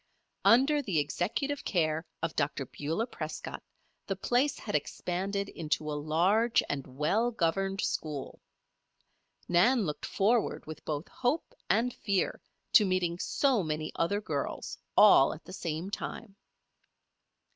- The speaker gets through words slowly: Yes, slow, 130 wpm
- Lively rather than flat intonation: Yes, wide, 6.1 semitones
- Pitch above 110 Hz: Yes, medium, 185 Hz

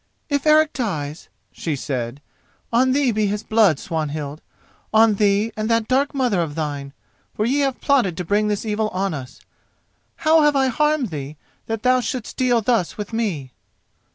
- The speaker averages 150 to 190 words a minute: Yes, average, 170 wpm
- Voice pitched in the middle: No, high, 215 Hz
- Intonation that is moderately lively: No, wide, 7.9 semitones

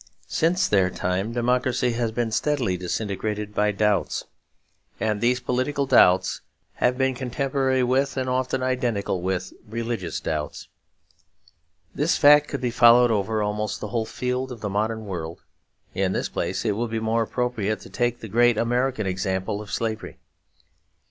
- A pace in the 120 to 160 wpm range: Yes, average, 155 wpm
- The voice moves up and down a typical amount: Yes, average, 3.4 semitones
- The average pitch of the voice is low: Yes, low, 115 Hz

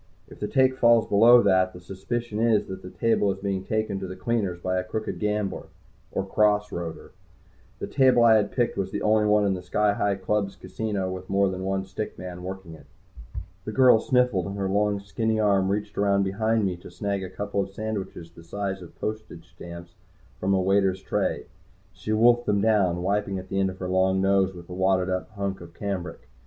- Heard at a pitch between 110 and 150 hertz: No, low, 100 Hz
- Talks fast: Yes, fast, 210 wpm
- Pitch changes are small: Yes, narrow, 2.2 semitones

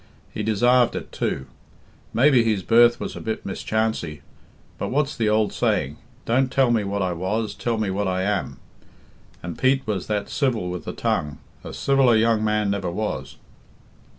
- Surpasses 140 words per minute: Yes, average, 175 wpm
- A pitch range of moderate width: Yes, average, 3.9 semitones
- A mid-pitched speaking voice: No, low, 110 Hz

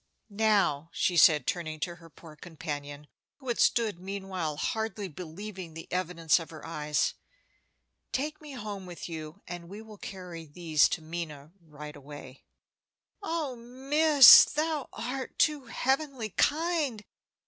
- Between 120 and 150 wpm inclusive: Yes, slow, 135 wpm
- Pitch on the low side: No, medium, 185 Hz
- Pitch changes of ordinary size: No, wide, 7.2 semitones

